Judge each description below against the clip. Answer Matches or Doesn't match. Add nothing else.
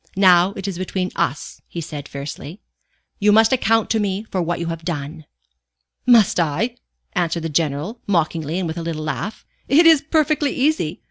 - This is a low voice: Doesn't match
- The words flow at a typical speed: Matches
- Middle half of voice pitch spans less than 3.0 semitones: Doesn't match